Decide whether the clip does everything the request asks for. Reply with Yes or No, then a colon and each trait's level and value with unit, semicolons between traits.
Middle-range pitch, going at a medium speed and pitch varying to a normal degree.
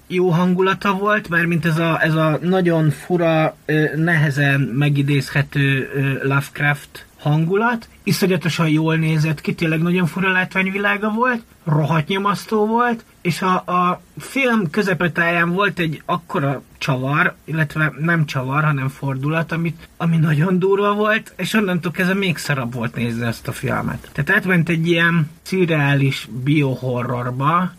Yes: medium, 165 Hz; average, 135 wpm; average, 3.9 semitones